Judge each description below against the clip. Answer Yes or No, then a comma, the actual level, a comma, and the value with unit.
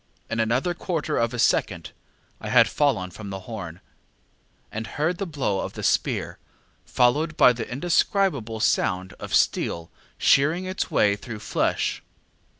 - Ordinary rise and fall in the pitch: No, wide, 6.8 semitones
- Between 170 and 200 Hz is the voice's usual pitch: No, low, 120 Hz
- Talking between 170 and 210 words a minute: No, average, 150 wpm